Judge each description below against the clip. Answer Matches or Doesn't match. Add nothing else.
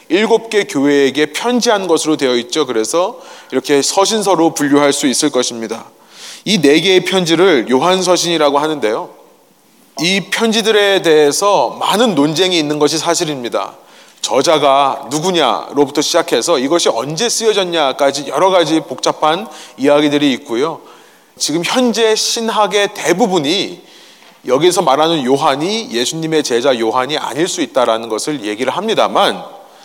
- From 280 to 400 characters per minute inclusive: Matches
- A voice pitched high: Doesn't match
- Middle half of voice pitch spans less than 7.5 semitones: Matches